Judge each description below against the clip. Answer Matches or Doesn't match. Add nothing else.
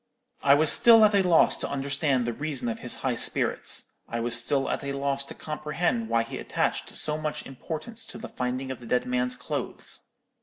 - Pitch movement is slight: Doesn't match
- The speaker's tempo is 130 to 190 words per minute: Doesn't match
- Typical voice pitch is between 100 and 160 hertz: Matches